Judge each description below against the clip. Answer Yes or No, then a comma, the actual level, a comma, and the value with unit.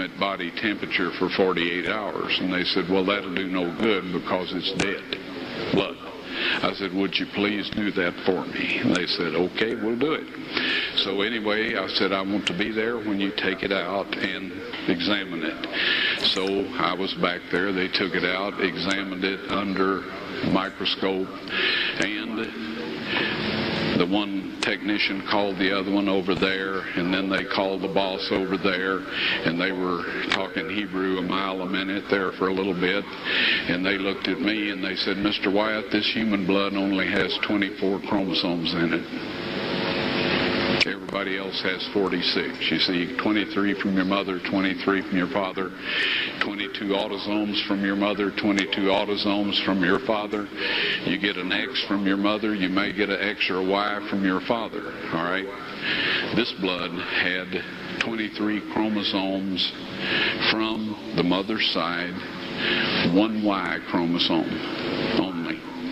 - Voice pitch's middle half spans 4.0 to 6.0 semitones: No, narrow, 1.4 semitones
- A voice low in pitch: Yes, very low, 95 Hz